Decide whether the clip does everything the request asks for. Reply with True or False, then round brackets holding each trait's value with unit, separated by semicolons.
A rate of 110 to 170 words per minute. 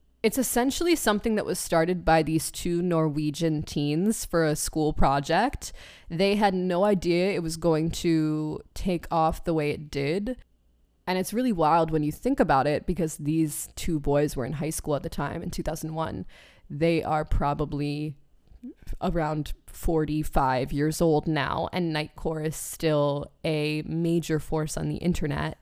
True (160 wpm)